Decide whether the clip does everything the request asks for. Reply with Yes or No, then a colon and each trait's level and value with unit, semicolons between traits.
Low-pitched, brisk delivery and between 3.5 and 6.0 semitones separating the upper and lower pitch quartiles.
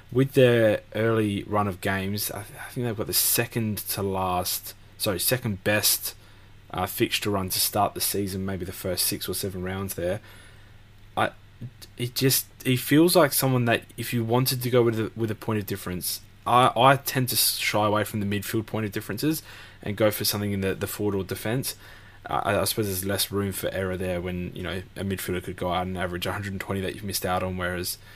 No: low, 100 Hz; fast, 215 wpm; narrow, 2.6 semitones